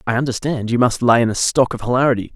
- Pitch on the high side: No, low, 120 Hz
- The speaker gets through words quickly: Yes, fast, 255 wpm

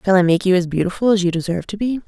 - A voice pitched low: No, high, 190 Hz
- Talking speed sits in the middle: No, fast, 320 wpm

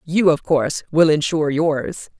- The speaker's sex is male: No, female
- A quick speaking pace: No, average, 165 wpm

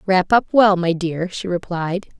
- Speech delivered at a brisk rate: No, average, 190 wpm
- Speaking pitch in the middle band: Yes, medium, 180 Hz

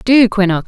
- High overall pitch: Yes, high, 210 Hz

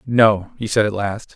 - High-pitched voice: No, low, 105 Hz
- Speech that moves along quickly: Yes, fast, 220 wpm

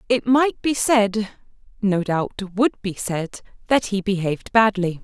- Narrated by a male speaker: No, female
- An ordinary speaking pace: Yes, average, 155 wpm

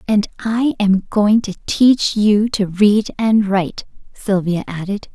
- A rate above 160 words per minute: No, average, 150 wpm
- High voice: Yes, high, 205 Hz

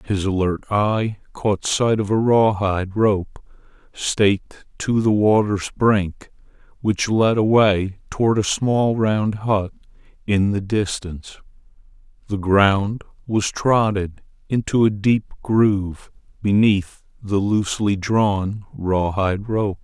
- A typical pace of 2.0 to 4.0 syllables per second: Yes, 3.6 syllables/s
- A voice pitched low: Yes, low, 105 Hz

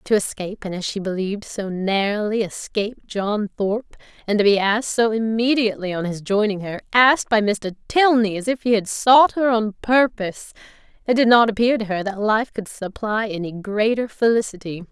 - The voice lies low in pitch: No, high, 215 Hz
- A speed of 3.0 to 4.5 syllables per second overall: No, 5.4 syllables/s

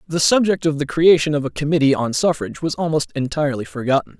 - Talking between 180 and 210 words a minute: Yes, average, 200 wpm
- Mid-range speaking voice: Yes, medium, 150 Hz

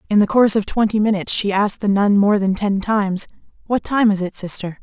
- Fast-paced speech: Yes, fast, 235 wpm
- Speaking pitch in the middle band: No, high, 205 Hz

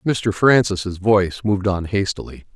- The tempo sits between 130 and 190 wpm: Yes, average, 140 wpm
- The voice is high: No, low, 100 Hz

